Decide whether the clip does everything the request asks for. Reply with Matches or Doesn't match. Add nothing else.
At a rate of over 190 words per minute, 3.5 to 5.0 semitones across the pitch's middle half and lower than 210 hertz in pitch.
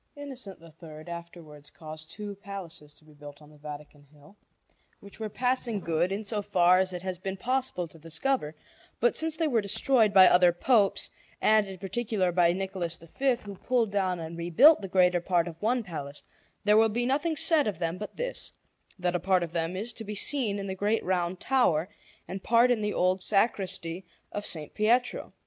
Matches